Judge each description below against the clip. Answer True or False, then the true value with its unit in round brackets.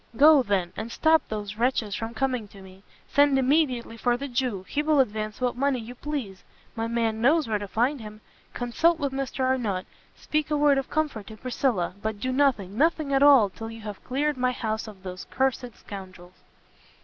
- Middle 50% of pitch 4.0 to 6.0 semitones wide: True (4.5 semitones)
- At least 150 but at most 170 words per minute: False (195 wpm)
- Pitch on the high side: True (245 Hz)